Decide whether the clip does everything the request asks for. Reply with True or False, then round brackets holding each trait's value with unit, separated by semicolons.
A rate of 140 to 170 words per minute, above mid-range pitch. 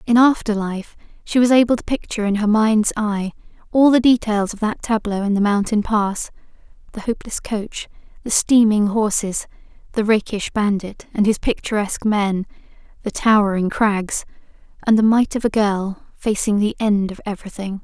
True (160 wpm; 210 Hz)